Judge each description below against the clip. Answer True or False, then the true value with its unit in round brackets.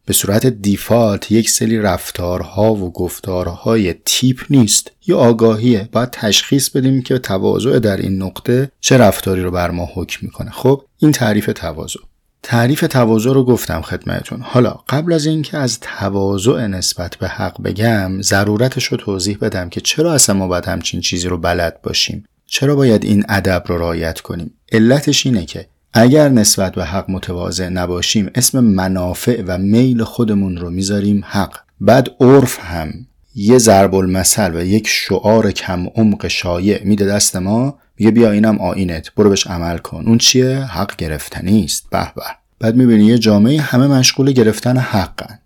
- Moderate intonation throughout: True (4.9 semitones)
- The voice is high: False (105 Hz)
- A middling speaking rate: False (160 wpm)